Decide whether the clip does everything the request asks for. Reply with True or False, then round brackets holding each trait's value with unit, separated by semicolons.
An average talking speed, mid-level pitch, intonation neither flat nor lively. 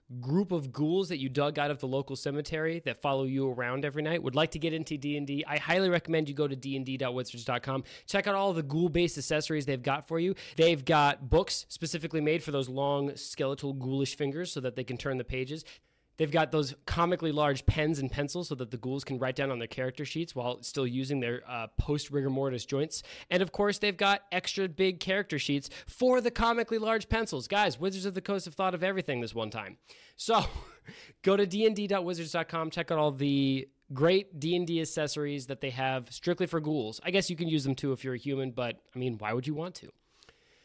False (220 wpm; 150 Hz; 4.3 semitones)